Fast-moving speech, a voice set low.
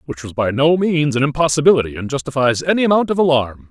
No: fast, 210 wpm; medium, 145 Hz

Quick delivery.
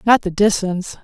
No: average, 175 wpm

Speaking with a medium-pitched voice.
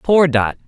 Yes: medium, 150 Hz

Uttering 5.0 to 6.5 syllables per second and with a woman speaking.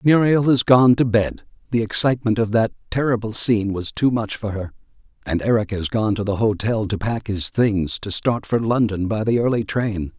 No: 5.1 syllables/s; male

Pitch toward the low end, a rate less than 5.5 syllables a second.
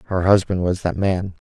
Yes: very low, 90 Hz; 5.2 syllables/s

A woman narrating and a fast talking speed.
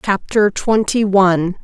No: female; slow, 110 wpm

